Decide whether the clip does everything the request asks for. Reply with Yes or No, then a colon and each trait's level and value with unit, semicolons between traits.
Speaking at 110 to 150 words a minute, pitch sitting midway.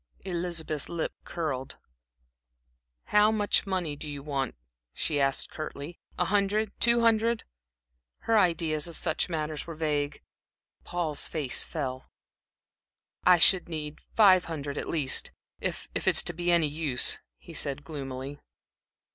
Yes: average, 140 wpm; medium, 160 Hz